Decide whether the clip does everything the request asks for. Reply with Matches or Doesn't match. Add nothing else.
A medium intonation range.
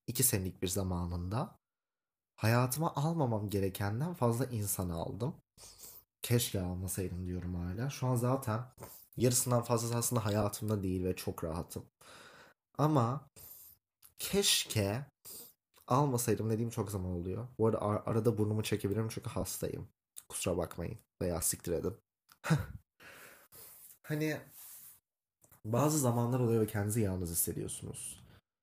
Matches